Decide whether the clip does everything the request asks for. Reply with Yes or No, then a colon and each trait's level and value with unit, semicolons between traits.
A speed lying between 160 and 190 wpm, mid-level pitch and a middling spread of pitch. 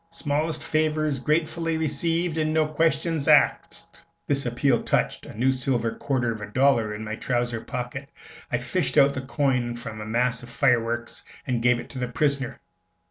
No: average, 175 wpm; low, 130 Hz; average, 4.3 semitones